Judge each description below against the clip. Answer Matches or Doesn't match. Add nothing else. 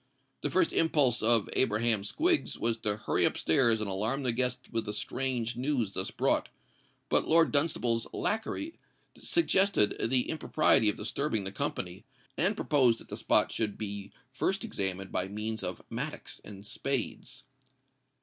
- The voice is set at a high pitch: Doesn't match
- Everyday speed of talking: Matches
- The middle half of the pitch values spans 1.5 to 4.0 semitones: Doesn't match